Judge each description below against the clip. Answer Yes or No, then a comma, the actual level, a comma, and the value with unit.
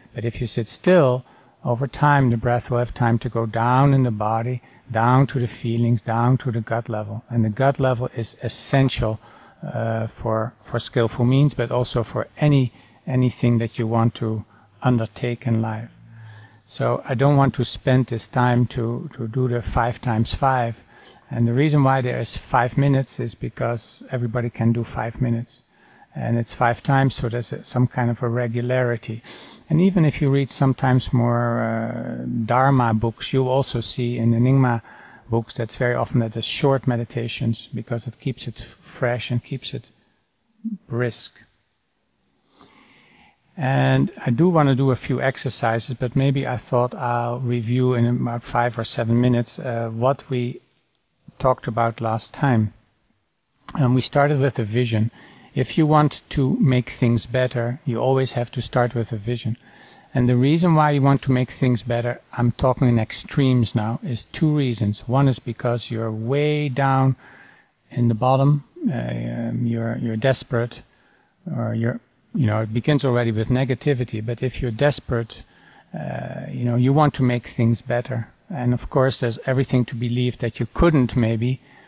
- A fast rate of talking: No, average, 175 wpm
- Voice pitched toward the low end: Yes, low, 120 Hz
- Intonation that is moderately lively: No, narrow, 2.3 semitones